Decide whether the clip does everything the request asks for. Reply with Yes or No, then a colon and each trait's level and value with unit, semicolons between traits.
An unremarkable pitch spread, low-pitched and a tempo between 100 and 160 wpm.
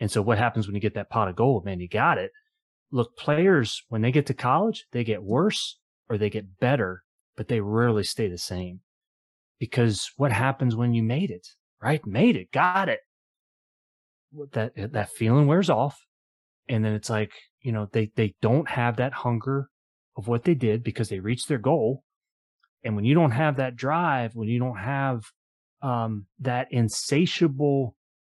No: average, 4.4 semitones; low, 120 Hz; average, 185 wpm